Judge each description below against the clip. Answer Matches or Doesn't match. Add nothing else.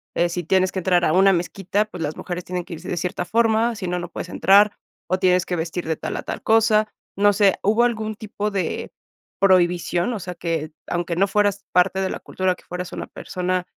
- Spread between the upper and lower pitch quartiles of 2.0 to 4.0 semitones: Matches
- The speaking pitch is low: Doesn't match